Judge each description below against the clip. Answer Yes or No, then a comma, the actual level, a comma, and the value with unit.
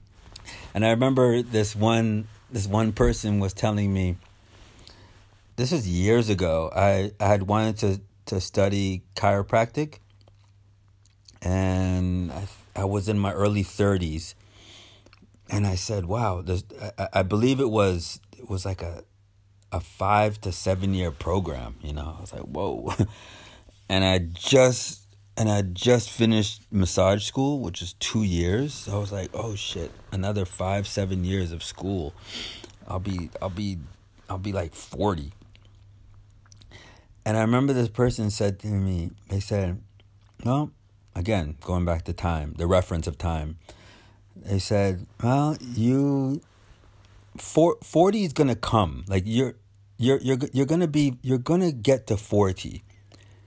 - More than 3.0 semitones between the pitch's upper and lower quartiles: No, narrow, 2.4 semitones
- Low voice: Yes, low, 100 Hz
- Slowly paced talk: No, average, 150 wpm